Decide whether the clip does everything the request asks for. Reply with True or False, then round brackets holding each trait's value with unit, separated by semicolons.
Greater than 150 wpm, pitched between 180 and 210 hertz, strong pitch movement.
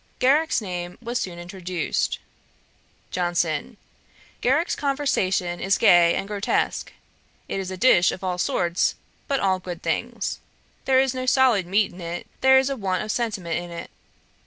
True (160 wpm; 190 Hz; 6.3 semitones)